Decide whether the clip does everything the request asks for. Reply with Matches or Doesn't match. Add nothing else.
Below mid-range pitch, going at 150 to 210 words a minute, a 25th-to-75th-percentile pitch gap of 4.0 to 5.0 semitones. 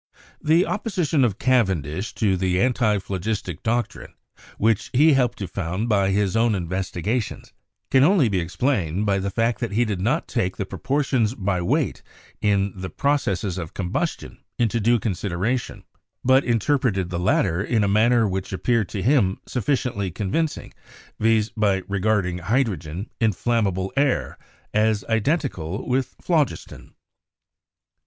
Doesn't match